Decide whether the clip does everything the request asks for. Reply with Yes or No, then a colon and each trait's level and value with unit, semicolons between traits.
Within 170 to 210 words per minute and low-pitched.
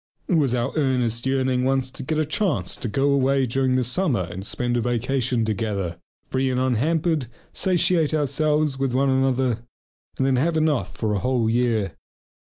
Yes: average, 175 wpm; low, 130 Hz